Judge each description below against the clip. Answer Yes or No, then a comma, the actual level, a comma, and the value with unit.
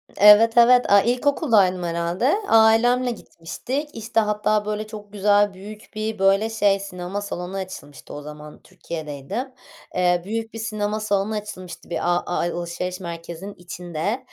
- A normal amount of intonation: Yes, average, 3.8 semitones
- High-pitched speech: Yes, high, 205 Hz